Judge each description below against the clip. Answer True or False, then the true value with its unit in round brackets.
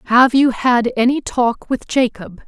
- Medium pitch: False (245 Hz)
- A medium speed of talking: True (170 wpm)